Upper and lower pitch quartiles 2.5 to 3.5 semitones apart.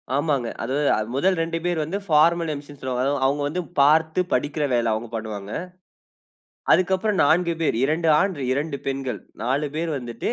No: average, 3.9 semitones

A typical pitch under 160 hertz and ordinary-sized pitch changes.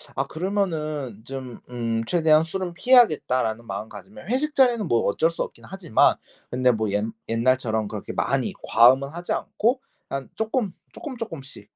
No: medium, 140 Hz; wide, 8.8 semitones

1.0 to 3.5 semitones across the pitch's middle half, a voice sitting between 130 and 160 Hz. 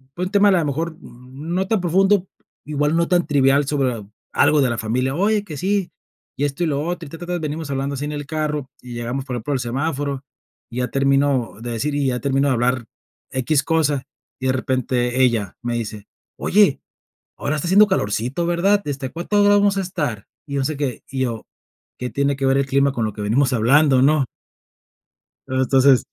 No: average, 4.2 semitones; medium, 140 Hz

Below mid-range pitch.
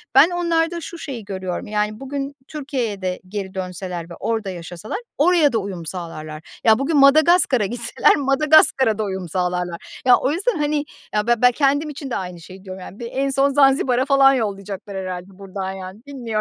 No: high, 225 Hz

